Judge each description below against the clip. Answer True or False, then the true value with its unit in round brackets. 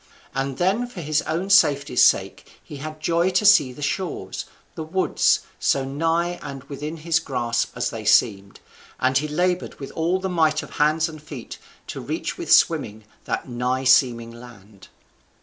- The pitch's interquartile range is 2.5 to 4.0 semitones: False (4.8 semitones)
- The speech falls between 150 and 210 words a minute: True (170 wpm)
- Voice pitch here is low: False (150 Hz)